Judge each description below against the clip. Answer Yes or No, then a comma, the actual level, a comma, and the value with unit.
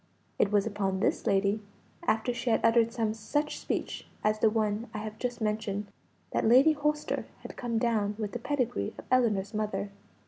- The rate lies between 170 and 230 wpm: Yes, average, 180 wpm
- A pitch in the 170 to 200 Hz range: No, high, 220 Hz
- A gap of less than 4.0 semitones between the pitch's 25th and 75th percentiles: Yes, narrow, 2.5 semitones